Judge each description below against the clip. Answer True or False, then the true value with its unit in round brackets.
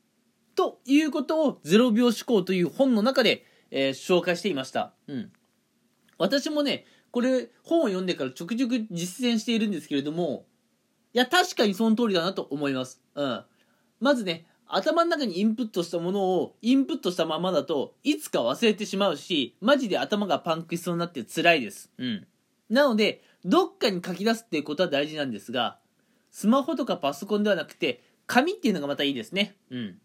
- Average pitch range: False (6.7 semitones)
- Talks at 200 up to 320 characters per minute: False (390 characters per minute)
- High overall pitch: True (210 Hz)